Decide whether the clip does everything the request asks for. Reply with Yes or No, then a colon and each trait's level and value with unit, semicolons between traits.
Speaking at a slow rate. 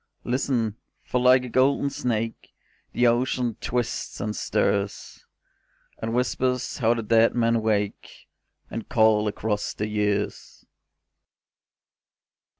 Yes: slow, 110 wpm